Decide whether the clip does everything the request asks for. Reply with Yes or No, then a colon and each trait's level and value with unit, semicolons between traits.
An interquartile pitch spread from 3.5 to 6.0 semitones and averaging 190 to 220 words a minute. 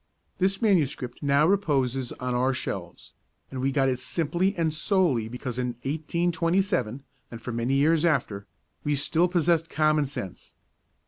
No: average, 4.9 semitones; average, 145 wpm